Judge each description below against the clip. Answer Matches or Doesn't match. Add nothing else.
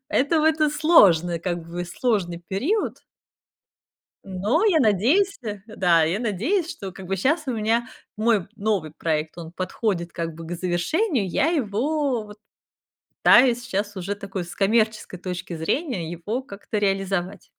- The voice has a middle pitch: Doesn't match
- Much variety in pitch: Matches